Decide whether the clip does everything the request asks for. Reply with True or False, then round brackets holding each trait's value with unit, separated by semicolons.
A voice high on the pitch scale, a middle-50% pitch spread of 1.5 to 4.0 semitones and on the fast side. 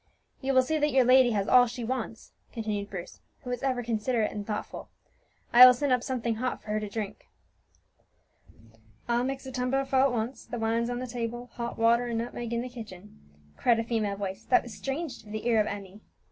True (235 Hz; 2.5 semitones; 215 wpm)